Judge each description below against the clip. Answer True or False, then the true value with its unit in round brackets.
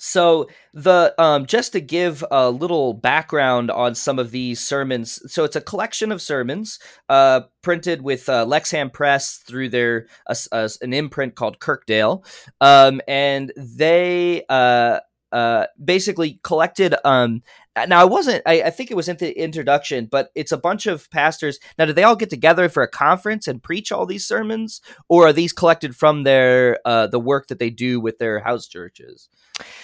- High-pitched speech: False (145 Hz)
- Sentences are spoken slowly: False (180 wpm)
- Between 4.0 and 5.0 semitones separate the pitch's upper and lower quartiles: False (5.5 semitones)